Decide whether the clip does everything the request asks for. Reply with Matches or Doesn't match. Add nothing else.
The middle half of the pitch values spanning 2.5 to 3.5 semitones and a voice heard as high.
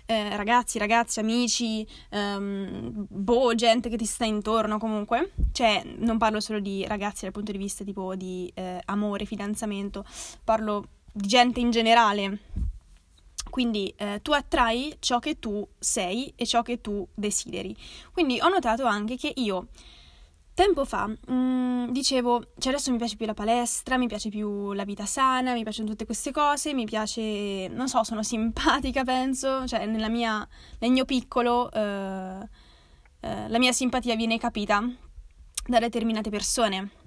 Matches